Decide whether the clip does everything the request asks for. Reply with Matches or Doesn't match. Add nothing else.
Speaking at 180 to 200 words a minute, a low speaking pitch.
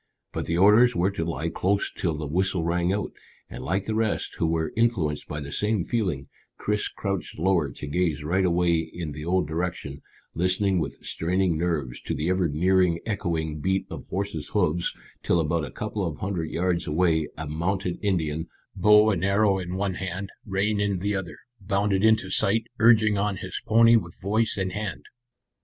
Matches